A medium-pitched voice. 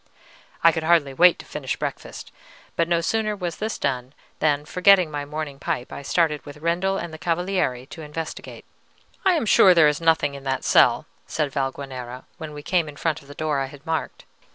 Yes: medium, 155 Hz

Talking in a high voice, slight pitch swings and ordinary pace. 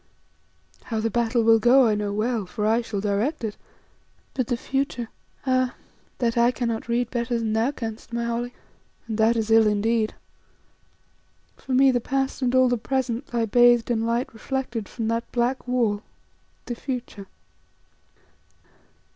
Yes: high, 235 Hz; narrow, 2.0 semitones; average, 160 wpm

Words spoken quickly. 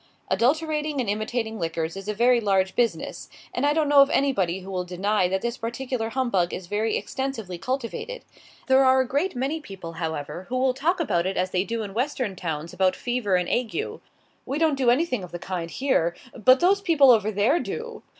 Yes: fast, 210 wpm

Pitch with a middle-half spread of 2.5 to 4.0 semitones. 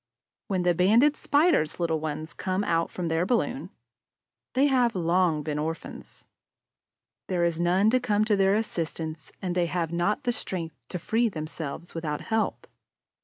No: average, 4.7 semitones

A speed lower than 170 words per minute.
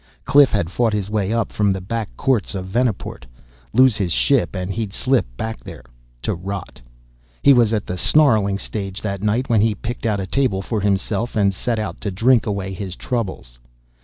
No: average, 195 wpm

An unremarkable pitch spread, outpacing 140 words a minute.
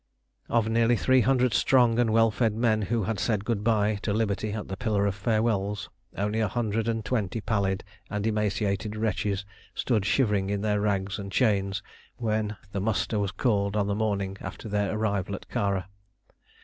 No: narrow, 2.0 semitones; average, 180 wpm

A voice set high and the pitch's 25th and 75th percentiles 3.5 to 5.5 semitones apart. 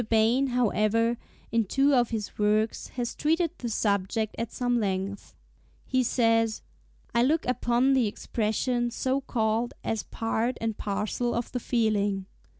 No: high, 230 Hz; narrow, 2.4 semitones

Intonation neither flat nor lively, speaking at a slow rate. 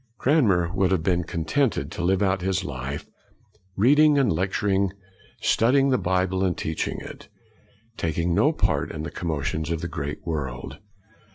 No: average, 3.6 semitones; average, 160 wpm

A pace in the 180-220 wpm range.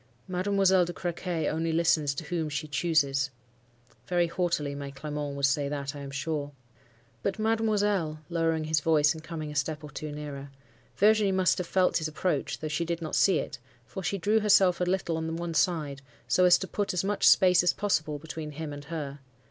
Yes: average, 195 wpm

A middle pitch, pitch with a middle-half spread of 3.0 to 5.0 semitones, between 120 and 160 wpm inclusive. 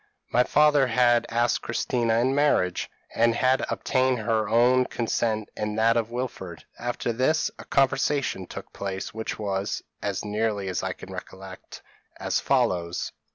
No: low, 115 Hz; average, 3.3 semitones; average, 155 wpm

